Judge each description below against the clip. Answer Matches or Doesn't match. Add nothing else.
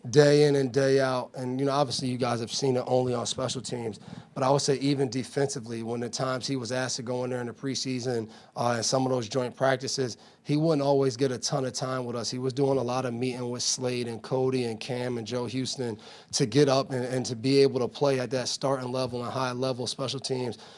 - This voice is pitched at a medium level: Doesn't match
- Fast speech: Matches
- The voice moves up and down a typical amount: Doesn't match